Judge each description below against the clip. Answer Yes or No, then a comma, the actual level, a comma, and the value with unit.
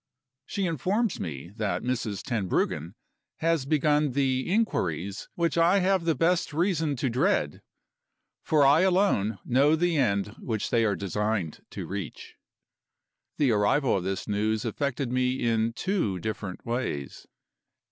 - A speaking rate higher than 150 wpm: No, slow, 135 wpm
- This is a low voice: Yes, low, 125 Hz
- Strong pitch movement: Yes, wide, 7.8 semitones